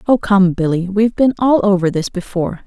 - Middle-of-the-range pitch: No, high, 195 Hz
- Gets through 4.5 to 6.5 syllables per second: Yes, 5.8 syllables/s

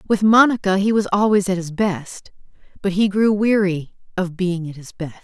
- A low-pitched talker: No, high, 190 Hz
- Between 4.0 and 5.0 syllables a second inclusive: Yes, 4.9 syllables/s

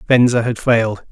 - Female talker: No, male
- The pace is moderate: Yes, average, 160 wpm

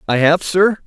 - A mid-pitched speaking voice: Yes, medium, 170 Hz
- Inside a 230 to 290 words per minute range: No, fast, 210 wpm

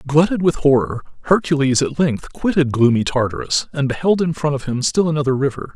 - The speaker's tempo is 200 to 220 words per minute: No, average, 190 wpm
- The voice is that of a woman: No, male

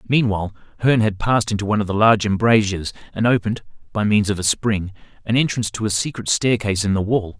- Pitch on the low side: Yes, low, 105 Hz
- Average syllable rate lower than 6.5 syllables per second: No, 7.0 syllables/s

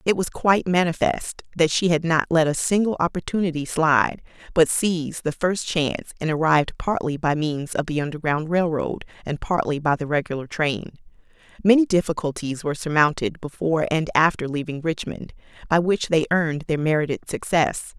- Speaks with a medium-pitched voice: Yes, medium, 160 Hz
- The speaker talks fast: No, average, 165 wpm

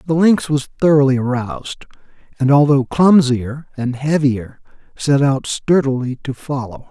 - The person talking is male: Yes, male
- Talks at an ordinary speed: No, slow, 130 wpm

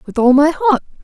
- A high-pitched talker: Yes, very high, 285 Hz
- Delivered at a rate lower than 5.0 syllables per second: No, 5.7 syllables/s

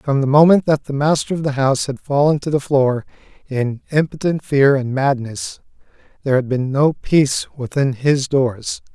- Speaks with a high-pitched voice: No, medium, 140 Hz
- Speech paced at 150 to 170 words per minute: No, average, 180 wpm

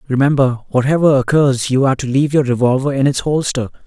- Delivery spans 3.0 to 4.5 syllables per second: No, 6.3 syllables/s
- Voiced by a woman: No, male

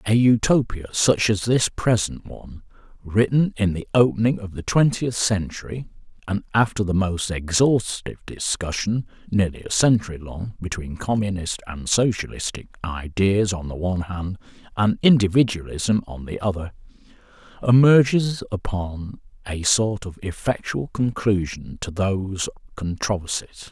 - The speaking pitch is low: Yes, low, 100 Hz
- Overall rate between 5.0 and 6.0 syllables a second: No, 4.6 syllables/s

